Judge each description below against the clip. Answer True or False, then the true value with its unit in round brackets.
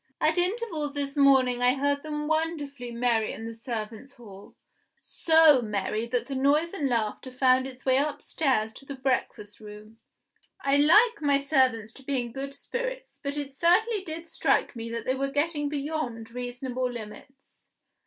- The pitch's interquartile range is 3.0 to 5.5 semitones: True (3.8 semitones)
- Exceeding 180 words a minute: False (165 wpm)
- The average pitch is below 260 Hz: False (270 Hz)